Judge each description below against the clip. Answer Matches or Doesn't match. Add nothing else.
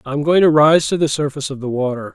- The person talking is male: Matches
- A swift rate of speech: Matches